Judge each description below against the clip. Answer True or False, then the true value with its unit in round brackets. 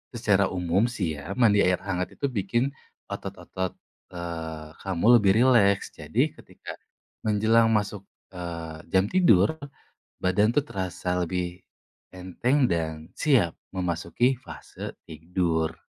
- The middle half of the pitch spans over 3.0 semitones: True (4.4 semitones)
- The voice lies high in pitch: False (95 Hz)